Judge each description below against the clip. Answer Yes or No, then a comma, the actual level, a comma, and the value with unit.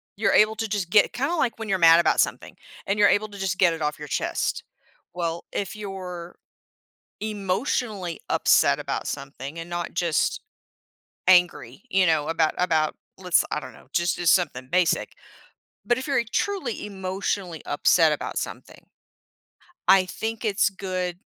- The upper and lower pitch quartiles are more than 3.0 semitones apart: Yes, average, 3.6 semitones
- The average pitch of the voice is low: No, medium, 185 Hz